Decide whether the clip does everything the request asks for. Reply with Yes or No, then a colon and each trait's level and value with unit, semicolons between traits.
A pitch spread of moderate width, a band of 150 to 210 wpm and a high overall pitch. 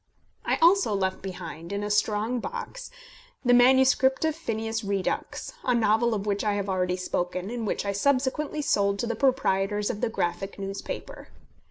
Yes: average, 4.4 semitones; average, 170 wpm; high, 210 Hz